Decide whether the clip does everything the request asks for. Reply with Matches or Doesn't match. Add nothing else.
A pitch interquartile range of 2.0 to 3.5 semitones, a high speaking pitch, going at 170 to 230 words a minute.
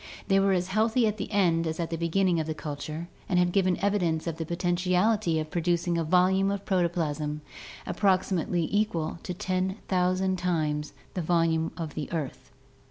Doesn't match